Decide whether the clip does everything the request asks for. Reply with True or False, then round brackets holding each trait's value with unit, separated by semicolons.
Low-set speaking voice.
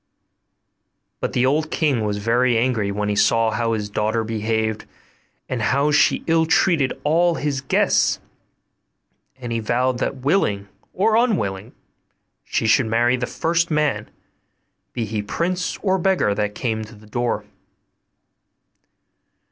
True (120 Hz)